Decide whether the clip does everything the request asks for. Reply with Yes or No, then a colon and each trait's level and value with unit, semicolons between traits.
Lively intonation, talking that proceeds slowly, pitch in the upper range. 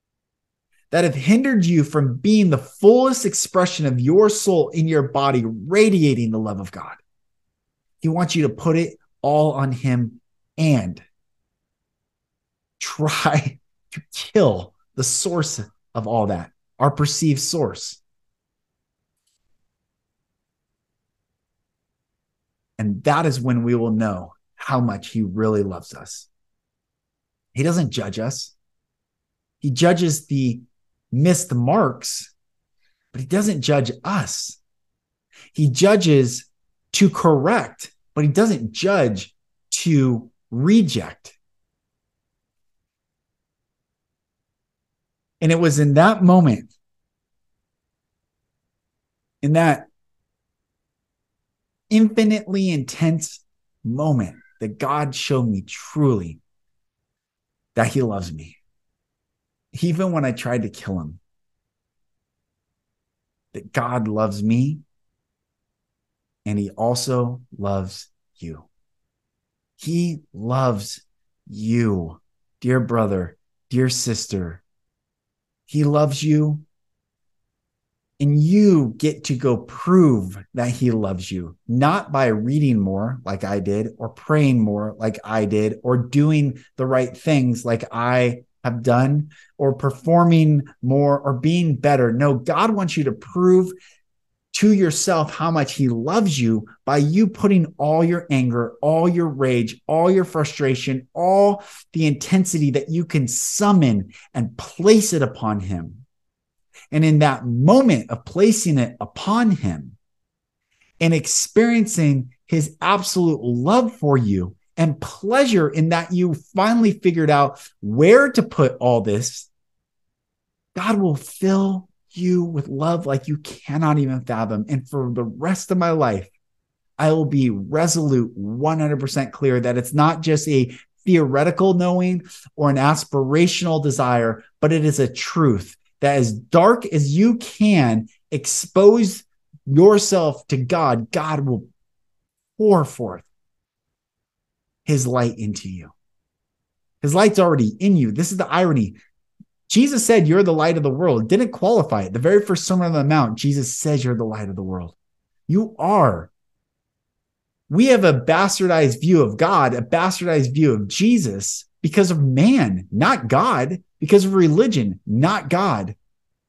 No: wide, 6.7 semitones; slow, 125 wpm; medium, 140 Hz